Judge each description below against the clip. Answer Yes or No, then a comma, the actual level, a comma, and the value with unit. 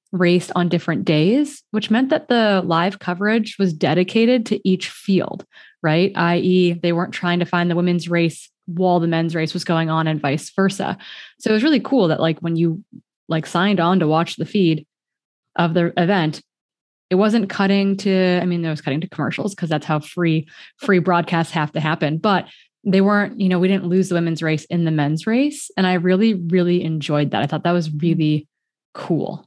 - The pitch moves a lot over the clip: No, average, 3.1 semitones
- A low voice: No, medium, 175 Hz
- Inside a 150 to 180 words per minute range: No, fast, 205 wpm